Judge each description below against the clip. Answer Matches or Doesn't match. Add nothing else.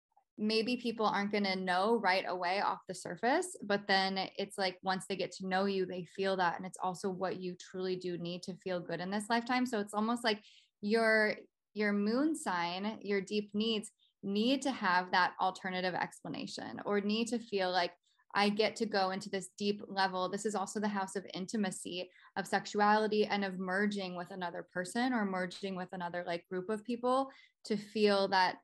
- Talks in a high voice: Matches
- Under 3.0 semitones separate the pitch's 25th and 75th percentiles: Matches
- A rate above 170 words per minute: Matches